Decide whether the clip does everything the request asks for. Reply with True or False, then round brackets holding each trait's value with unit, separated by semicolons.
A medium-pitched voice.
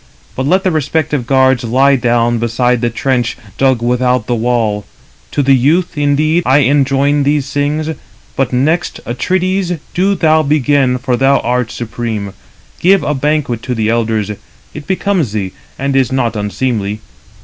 False (130 Hz)